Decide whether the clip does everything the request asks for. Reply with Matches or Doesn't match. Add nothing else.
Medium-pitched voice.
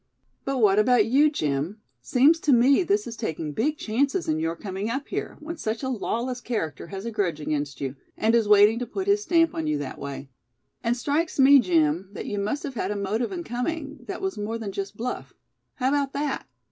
Doesn't match